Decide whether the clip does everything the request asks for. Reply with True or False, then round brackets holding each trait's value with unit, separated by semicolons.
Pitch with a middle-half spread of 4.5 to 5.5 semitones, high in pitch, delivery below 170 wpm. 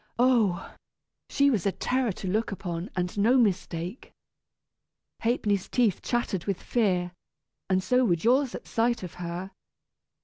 True (5.0 semitones; 200 Hz; 140 wpm)